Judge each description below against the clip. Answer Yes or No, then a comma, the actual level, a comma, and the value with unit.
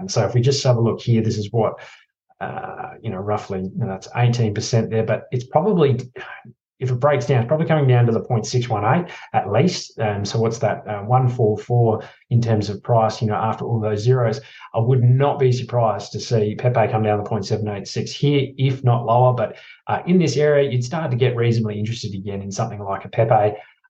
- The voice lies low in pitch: Yes, low, 115 Hz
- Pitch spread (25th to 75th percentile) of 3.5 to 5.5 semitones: No, average, 3.1 semitones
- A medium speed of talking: No, fast, 215 wpm